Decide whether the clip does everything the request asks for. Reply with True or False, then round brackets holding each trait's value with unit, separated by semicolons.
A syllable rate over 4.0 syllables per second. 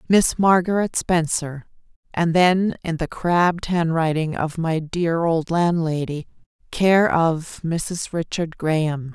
False (3.6 syllables/s)